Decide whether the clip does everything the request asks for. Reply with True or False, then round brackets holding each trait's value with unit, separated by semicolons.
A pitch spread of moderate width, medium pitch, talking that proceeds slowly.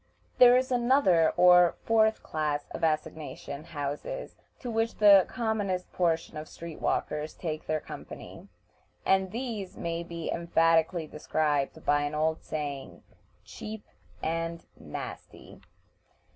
True (4.9 semitones; 165 Hz; 120 wpm)